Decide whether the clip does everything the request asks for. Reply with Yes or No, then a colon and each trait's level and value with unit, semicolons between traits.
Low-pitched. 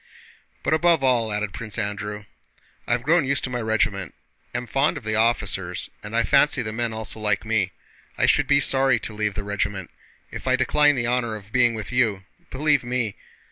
Yes: low, 115 Hz